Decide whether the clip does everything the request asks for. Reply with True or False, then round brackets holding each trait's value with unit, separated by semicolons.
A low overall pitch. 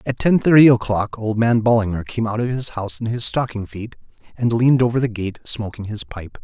True (115 Hz)